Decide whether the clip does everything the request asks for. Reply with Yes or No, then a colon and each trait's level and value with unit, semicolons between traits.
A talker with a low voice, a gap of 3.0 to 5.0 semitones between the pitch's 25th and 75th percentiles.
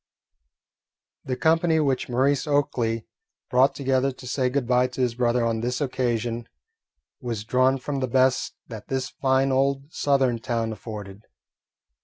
No: low, 130 Hz; narrow, 2.4 semitones